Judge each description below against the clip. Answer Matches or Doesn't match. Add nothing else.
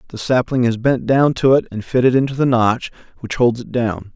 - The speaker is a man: Matches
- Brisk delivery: Matches